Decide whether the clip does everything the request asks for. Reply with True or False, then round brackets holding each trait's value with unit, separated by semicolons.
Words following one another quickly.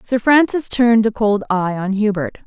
False (195 wpm)